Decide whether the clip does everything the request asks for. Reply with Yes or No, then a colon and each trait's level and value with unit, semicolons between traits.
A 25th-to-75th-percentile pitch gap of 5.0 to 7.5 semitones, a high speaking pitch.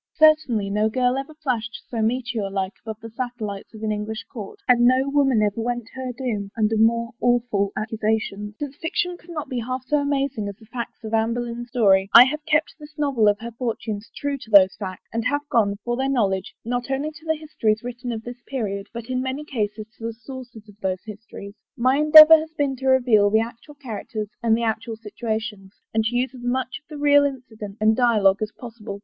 No: average, 3.5 semitones; high, 235 Hz